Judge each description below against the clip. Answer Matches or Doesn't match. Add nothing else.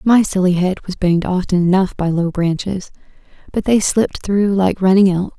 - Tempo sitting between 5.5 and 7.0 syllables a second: Doesn't match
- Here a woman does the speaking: Matches